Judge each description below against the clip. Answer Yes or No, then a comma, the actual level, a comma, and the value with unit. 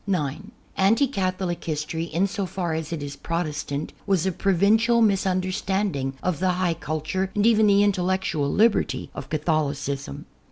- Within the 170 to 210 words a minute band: No, average, 150 wpm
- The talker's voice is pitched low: No, medium, 185 Hz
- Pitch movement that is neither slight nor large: Yes, average, 4.1 semitones